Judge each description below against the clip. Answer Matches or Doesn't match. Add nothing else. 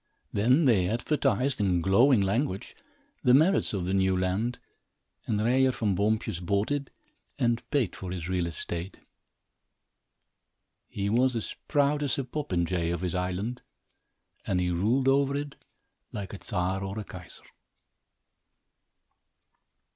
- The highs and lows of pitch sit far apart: Matches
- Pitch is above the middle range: Doesn't match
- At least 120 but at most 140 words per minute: Matches